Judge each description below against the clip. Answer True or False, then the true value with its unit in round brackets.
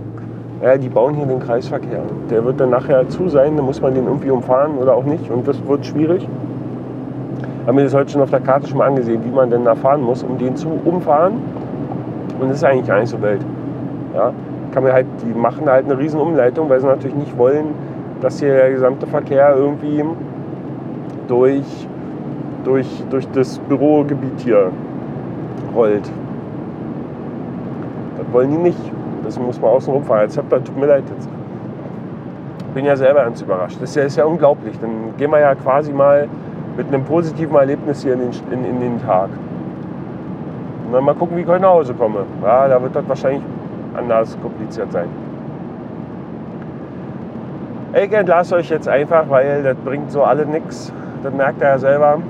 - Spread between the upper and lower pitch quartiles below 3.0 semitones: True (2.4 semitones)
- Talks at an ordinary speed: True (175 wpm)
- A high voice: False (140 Hz)